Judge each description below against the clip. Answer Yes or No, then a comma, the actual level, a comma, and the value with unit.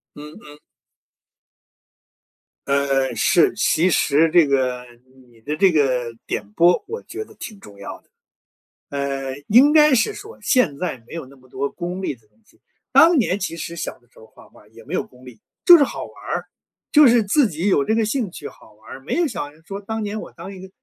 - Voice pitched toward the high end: No, medium, 170 Hz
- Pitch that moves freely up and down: Yes, wide, 8.3 semitones